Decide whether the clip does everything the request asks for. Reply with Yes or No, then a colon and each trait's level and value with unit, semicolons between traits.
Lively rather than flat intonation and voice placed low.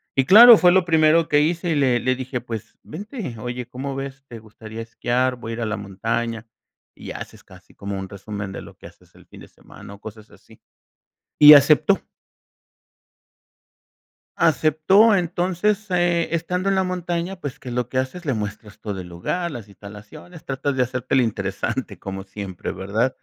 Yes: wide, 7.5 semitones; low, 130 Hz